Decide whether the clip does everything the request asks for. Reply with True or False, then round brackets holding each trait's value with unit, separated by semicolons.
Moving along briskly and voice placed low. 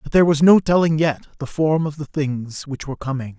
False (250 wpm; 150 Hz)